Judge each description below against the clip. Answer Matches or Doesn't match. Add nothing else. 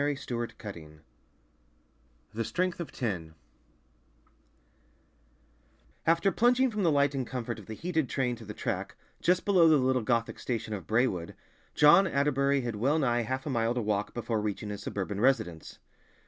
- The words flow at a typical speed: Matches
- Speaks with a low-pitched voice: Matches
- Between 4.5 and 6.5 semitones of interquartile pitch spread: Matches